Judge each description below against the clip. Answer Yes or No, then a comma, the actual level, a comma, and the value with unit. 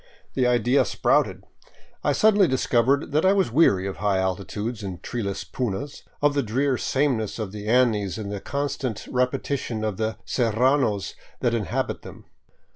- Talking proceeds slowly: No, average, 155 wpm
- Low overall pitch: Yes, low, 120 Hz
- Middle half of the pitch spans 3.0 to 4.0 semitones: No, average, 4.7 semitones